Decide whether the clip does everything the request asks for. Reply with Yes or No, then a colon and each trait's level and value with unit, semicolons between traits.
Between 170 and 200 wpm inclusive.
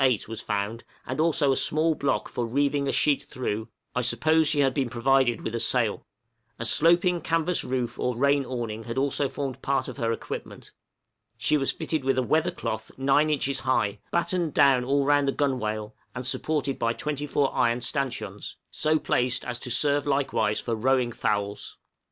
Yes: average, 180 wpm